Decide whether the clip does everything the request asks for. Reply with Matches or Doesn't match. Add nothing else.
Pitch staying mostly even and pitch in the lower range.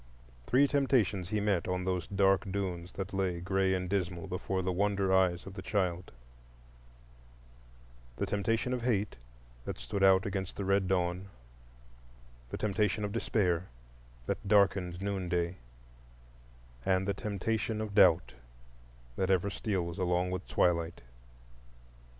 Matches